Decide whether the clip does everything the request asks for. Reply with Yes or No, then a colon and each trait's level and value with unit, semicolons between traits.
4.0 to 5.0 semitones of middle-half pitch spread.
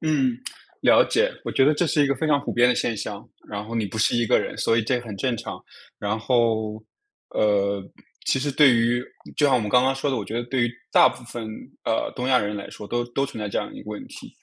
No: average, 3.6 semitones